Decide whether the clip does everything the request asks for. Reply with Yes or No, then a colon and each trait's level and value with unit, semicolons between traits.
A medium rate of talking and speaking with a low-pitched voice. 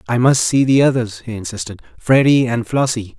Yes: average, 190 wpm; low, 120 Hz